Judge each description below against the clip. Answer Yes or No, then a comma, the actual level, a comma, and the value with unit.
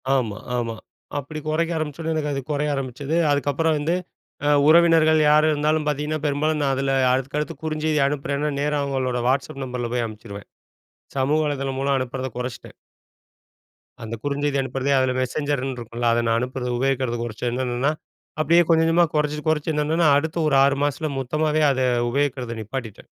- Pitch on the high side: No, medium, 140 Hz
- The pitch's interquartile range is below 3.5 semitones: Yes, average, 3.1 semitones